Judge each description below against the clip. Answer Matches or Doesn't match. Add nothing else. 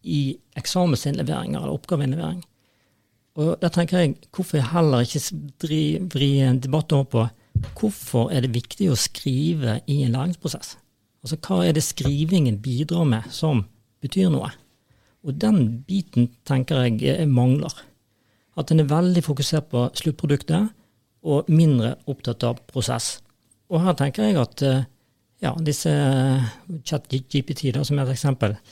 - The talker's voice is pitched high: Doesn't match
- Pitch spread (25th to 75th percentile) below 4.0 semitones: Doesn't match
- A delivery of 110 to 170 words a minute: Matches